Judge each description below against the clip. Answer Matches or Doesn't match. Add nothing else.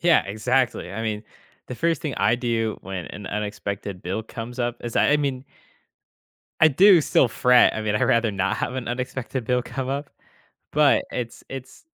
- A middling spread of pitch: Matches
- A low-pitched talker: Matches